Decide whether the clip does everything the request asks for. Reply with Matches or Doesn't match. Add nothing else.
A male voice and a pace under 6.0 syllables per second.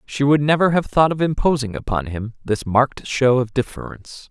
Matches